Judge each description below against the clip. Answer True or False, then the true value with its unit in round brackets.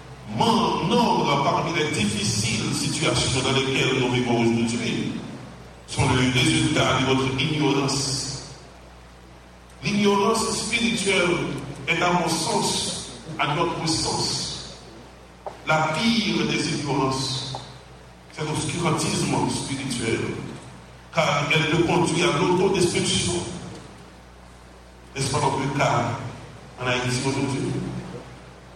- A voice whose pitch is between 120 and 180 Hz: True (135 Hz)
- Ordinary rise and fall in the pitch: False (6.0 semitones)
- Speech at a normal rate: False (95 wpm)